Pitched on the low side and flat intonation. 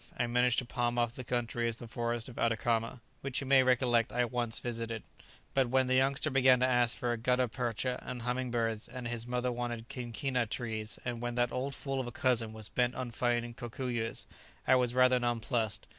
Yes: low, 120 Hz; narrow, 1.4 semitones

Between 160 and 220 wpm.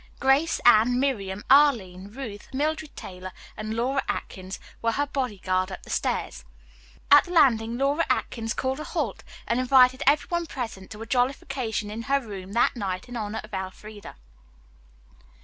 Yes: average, 165 wpm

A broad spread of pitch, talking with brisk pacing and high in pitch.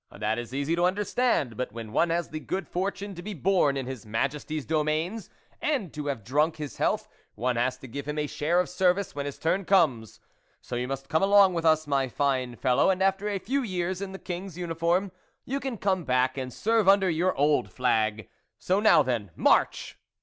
No: wide, 6.3 semitones; fast, 210 wpm; medium, 160 Hz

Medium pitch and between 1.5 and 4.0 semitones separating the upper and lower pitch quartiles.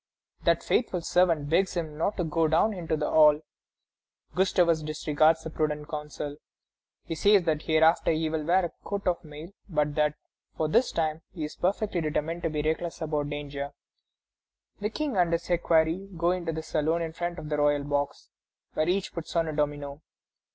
Yes: medium, 160 Hz; narrow, 2.4 semitones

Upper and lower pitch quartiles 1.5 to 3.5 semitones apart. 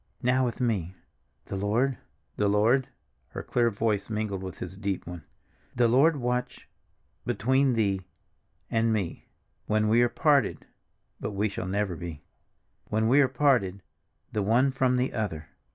No: average, 4.3 semitones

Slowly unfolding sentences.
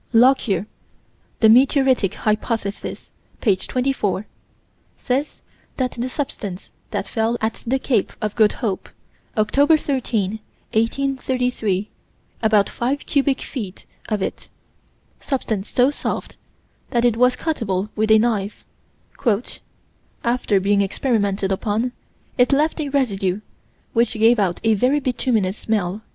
Yes: slow, 120 wpm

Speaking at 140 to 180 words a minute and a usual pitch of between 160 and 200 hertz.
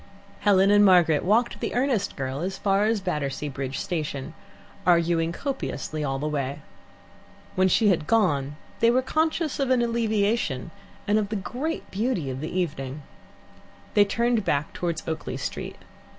Yes: average, 155 wpm; medium, 185 Hz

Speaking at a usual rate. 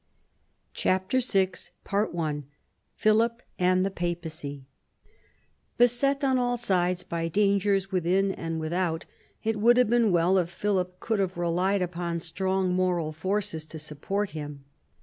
No: slow, 130 wpm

